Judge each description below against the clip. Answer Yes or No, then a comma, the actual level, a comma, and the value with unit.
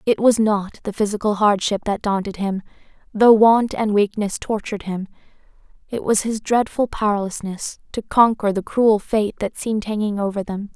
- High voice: Yes, high, 210 Hz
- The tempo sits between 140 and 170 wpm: Yes, average, 165 wpm